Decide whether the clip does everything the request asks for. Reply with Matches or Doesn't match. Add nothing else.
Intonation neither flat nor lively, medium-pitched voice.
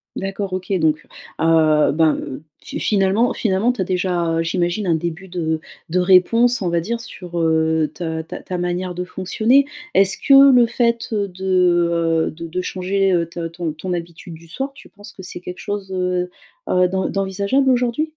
Matches